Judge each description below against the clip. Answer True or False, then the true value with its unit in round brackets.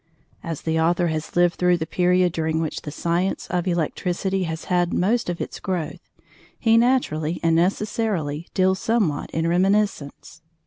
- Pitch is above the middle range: False (175 Hz)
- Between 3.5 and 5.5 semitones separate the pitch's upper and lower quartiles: False (2.7 semitones)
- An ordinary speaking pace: True (155 wpm)